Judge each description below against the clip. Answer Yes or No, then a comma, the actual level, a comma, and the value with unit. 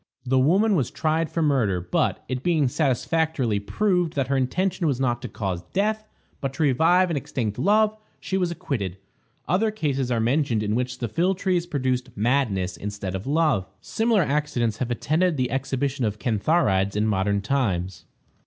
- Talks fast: No, average, 170 wpm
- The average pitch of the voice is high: No, low, 135 Hz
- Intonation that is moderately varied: No, wide, 6.9 semitones